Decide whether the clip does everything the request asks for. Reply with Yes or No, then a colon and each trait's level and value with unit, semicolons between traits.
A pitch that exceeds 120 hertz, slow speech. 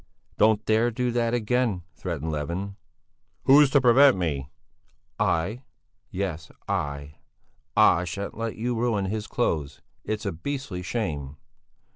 No: low, 105 Hz; slow, 130 wpm